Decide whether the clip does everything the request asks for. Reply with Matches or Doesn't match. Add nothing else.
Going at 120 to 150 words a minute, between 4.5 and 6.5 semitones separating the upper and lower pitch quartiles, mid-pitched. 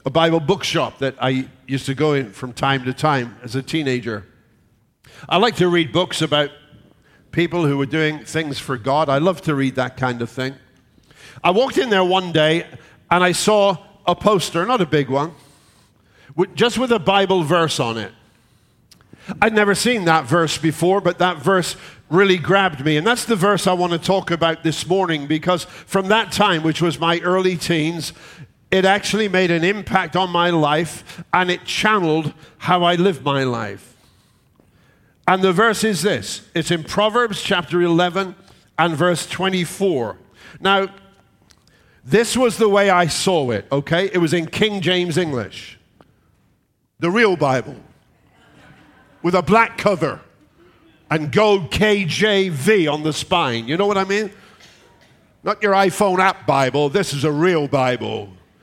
Doesn't match